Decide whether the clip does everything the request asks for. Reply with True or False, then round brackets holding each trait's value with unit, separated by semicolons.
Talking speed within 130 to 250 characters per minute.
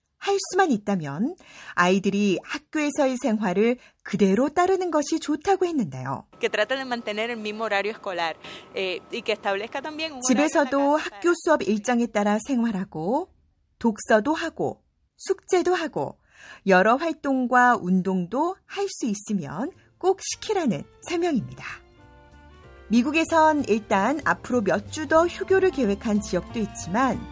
True (235 characters per minute)